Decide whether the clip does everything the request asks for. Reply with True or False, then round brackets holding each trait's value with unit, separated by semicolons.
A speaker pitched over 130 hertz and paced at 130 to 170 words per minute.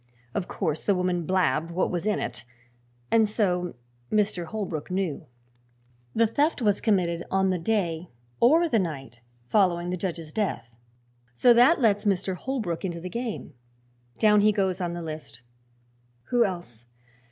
True (185 Hz; 150 wpm)